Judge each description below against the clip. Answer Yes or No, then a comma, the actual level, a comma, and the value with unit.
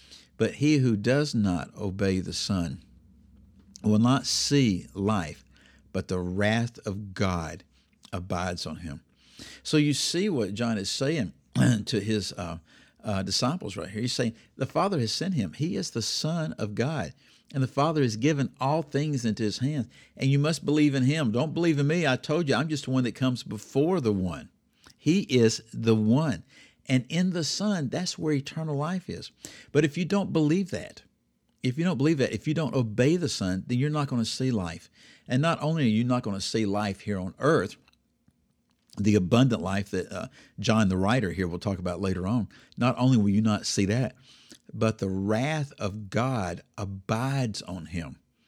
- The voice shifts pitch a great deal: Yes, wide, 6.3 semitones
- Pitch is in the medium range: No, low, 115 Hz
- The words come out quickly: No, average, 195 wpm